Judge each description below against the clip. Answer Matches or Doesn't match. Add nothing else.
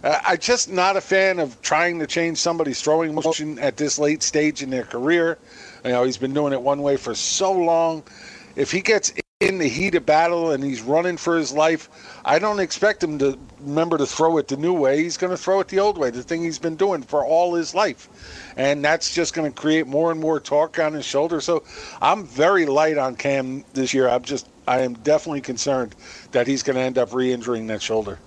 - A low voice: Doesn't match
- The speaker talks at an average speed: Doesn't match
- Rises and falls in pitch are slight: Doesn't match